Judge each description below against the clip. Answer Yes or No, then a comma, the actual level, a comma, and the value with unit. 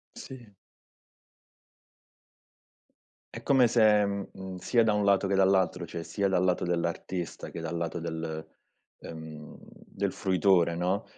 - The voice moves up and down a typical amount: Yes, average, 3.0 semitones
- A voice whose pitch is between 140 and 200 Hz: No, very low, 95 Hz